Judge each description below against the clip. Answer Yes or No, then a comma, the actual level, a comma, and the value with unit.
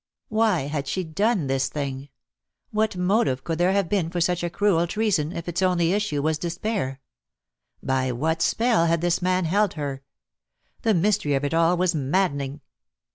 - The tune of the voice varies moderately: Yes, average, 4.7 semitones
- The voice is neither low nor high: Yes, medium, 170 Hz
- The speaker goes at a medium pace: Yes, average, 170 wpm